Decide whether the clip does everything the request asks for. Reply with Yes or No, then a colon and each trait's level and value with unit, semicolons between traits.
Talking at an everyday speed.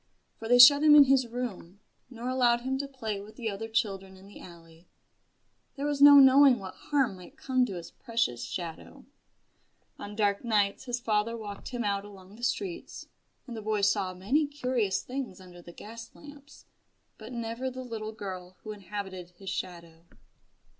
Yes: average, 180 wpm